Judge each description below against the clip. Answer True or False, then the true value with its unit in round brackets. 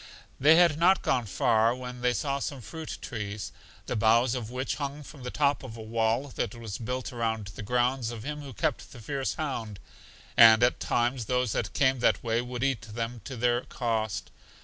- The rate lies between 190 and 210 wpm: True (200 wpm)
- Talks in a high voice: False (120 Hz)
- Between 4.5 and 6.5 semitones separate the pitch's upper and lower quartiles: False (3.0 semitones)